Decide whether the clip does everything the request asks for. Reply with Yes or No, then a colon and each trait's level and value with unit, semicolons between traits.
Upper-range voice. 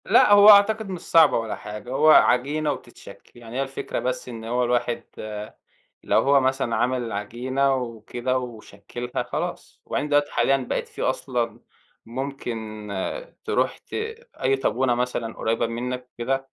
No: low, 125 Hz